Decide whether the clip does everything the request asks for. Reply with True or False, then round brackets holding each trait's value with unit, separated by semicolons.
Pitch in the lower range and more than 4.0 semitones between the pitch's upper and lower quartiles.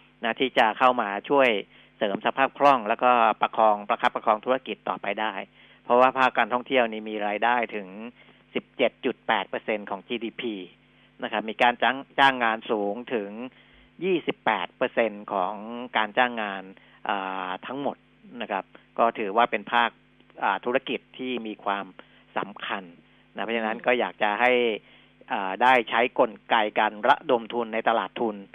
False (115 Hz; 3.1 semitones)